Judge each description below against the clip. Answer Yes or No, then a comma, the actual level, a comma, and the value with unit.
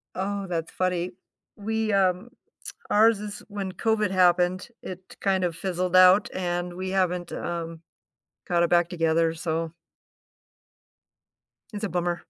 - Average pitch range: No, narrow, 2.1 semitones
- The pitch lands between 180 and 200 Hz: Yes, medium, 185 Hz